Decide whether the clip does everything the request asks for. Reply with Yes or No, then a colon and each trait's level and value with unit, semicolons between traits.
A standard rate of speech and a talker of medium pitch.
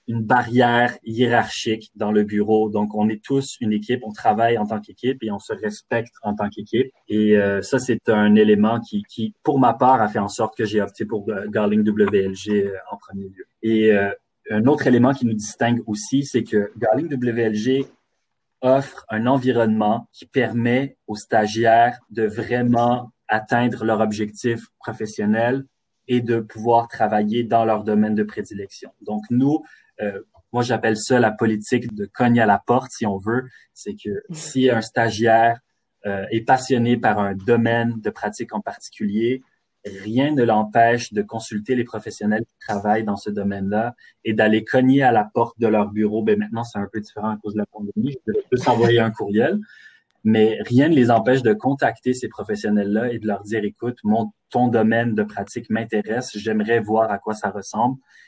No: average, 180 wpm; low, 110 Hz